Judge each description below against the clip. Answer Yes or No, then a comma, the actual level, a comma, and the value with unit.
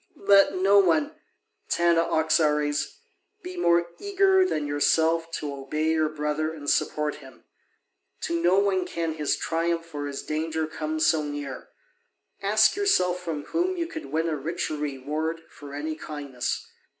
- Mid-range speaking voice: Yes, medium, 160 Hz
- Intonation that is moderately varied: Yes, average, 3.1 semitones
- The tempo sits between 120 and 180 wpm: Yes, average, 145 wpm